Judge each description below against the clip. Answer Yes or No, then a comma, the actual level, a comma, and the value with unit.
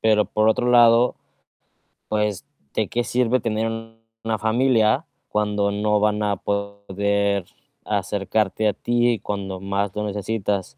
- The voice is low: Yes, low, 105 Hz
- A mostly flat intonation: Yes, narrow, 1.7 semitones